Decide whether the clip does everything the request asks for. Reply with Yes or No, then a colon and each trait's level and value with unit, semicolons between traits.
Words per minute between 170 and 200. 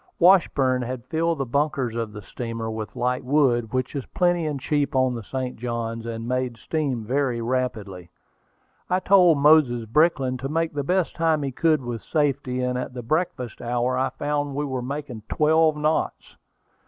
Yes: average, 180 wpm